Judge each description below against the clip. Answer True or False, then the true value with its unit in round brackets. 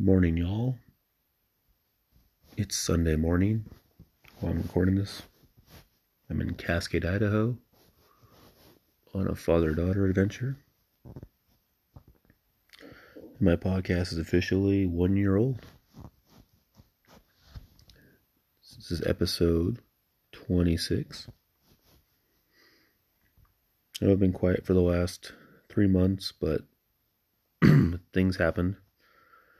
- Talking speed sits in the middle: False (85 wpm)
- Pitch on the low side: True (95 Hz)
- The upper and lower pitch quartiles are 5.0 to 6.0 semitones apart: False (3.1 semitones)